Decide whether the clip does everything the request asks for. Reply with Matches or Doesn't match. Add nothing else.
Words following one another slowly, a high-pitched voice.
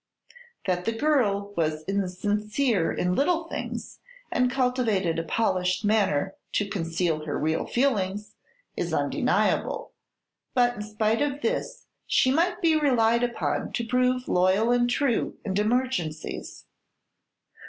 Matches